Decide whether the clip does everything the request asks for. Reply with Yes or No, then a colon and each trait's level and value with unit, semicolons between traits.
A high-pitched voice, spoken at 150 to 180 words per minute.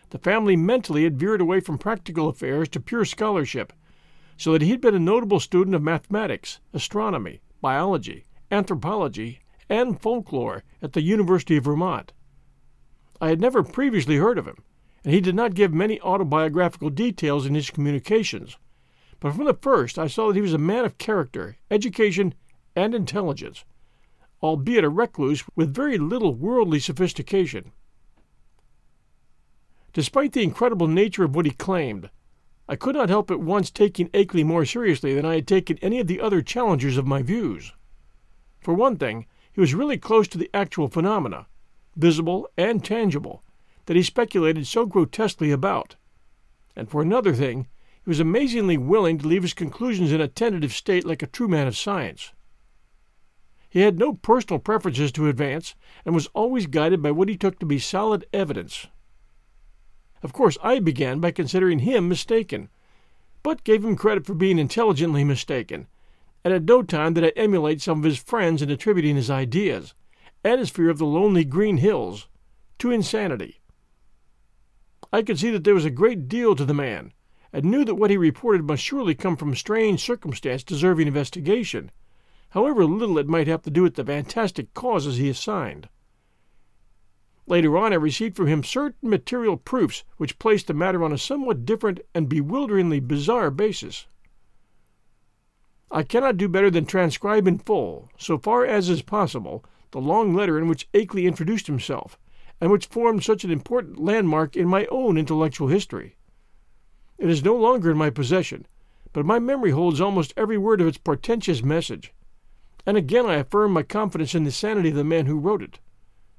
No: medium, 175 Hz; average, 170 wpm